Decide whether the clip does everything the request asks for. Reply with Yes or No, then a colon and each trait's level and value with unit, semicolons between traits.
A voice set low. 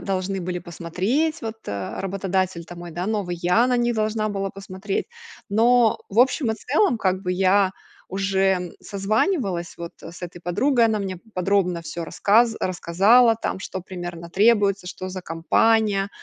No: high, 195 Hz